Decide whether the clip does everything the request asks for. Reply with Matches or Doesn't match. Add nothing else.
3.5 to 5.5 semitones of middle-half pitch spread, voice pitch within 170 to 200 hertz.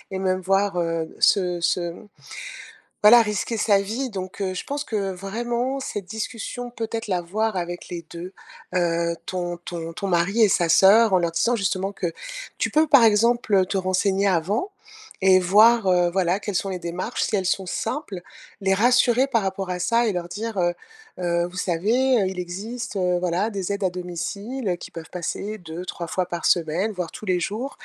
Matches